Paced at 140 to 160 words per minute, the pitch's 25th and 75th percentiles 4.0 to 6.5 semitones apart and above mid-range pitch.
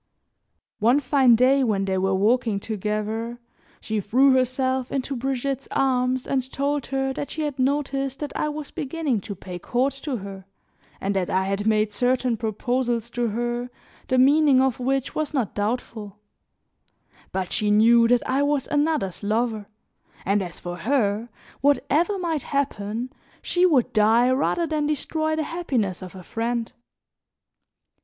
Yes: average, 155 wpm; average, 4.5 semitones; very high, 250 Hz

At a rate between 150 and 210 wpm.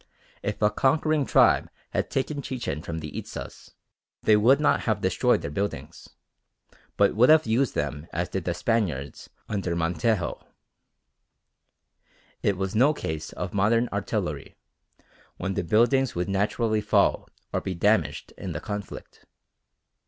No: average, 140 wpm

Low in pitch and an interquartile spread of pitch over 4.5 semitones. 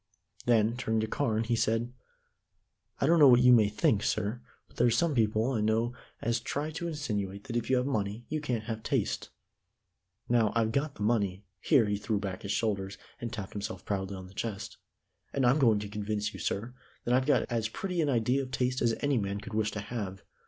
No: low, 115 Hz; average, 3.2 semitones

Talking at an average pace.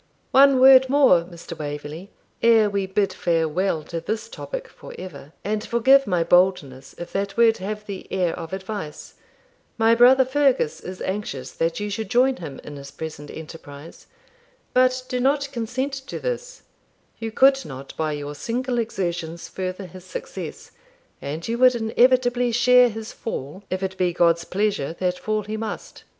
Yes: average, 165 wpm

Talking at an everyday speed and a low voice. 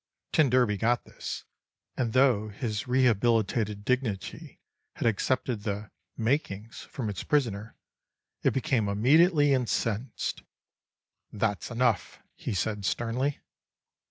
No: slow, 105 wpm; low, 115 Hz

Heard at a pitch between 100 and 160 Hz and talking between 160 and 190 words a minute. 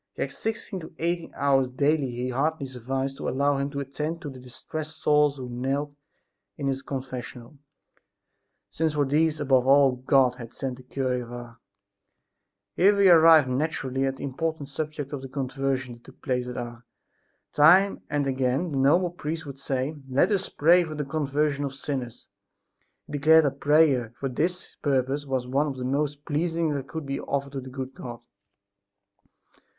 Yes: medium, 140 Hz; average, 175 wpm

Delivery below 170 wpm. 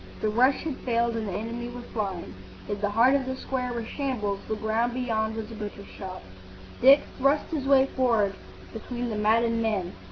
No: average, 195 wpm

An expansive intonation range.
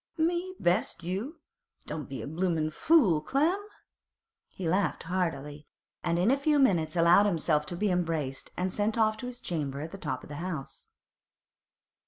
Yes: wide, 6.2 semitones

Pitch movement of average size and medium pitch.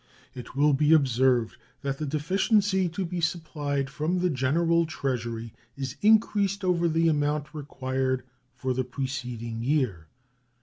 Yes: average, 4.4 semitones; medium, 145 Hz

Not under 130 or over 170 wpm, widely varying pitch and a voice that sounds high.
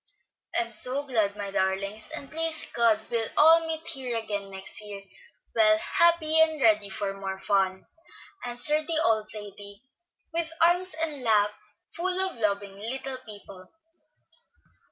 Yes: average, 145 wpm; wide, 7.4 semitones; high, 225 Hz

